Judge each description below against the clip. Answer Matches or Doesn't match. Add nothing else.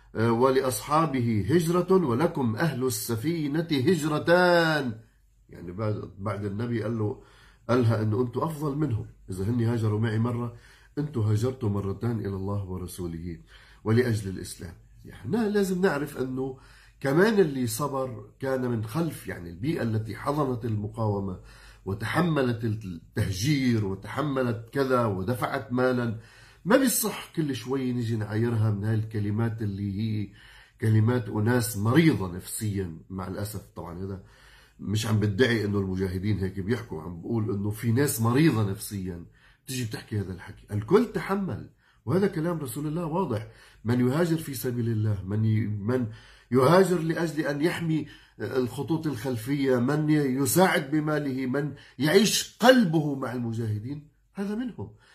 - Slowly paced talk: Doesn't match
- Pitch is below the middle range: Matches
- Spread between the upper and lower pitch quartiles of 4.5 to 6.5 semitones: Matches